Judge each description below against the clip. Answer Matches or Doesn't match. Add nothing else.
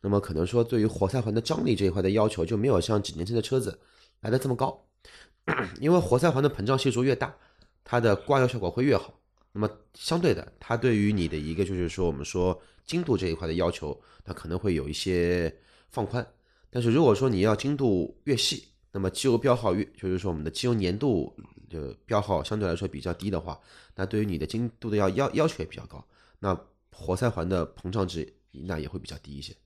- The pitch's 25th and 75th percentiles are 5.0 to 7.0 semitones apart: Matches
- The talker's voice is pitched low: Matches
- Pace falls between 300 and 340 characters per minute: Matches